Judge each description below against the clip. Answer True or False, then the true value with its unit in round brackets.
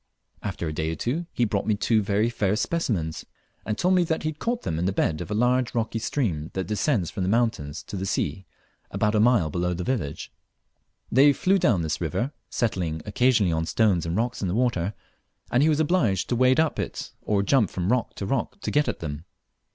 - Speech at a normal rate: False (220 wpm)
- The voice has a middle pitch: False (105 Hz)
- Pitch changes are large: True (6.2 semitones)